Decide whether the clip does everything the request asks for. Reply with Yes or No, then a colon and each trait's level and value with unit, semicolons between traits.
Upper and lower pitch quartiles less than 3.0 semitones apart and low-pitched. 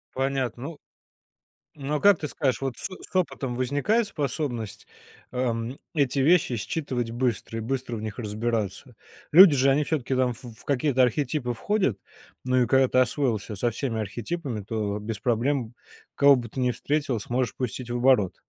No: average, 3.4 semitones; low, 125 Hz